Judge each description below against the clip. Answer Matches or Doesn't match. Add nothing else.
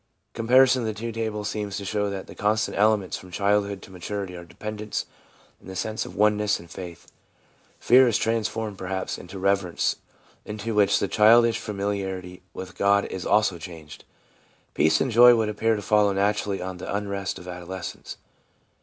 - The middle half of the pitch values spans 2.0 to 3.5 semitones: Matches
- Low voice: Matches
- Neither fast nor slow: Matches